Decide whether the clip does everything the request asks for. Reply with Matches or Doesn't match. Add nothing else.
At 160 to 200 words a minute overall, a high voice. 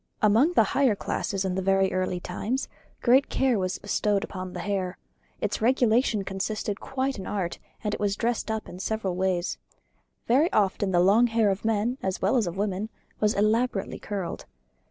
Matches